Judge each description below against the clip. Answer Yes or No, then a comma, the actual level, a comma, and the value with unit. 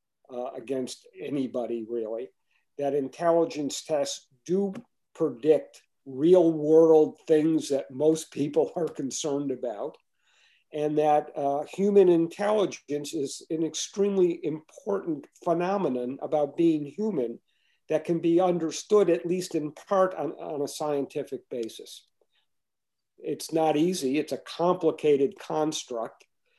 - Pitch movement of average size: Yes, average, 3.9 semitones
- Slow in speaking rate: Yes, slow, 115 wpm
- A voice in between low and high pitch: Yes, medium, 155 Hz